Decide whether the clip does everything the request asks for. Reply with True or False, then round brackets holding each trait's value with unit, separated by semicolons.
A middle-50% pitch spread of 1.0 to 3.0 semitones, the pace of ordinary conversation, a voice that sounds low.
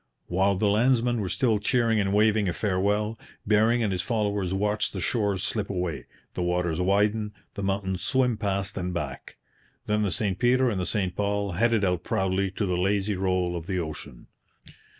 True (2.6 semitones; 185 wpm; 100 Hz)